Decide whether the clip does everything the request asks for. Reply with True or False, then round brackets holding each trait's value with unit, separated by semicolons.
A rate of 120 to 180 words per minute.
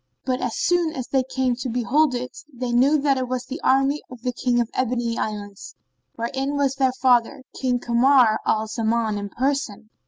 False (195 wpm)